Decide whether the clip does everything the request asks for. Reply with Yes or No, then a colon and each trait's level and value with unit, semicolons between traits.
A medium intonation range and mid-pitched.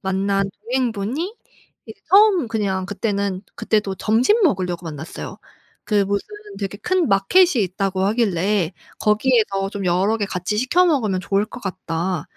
No: average, 3.5 semitones; high, 200 Hz